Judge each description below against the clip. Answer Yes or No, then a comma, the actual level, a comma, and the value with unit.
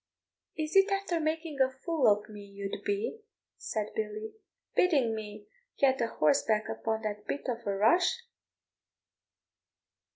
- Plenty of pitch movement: Yes, wide, 7.4 semitones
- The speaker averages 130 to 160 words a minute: Yes, slow, 135 wpm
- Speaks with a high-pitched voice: Yes, high, 235 Hz